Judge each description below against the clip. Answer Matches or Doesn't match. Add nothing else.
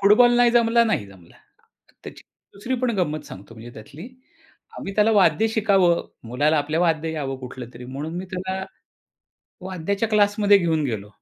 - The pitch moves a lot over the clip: Matches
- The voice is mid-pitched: Matches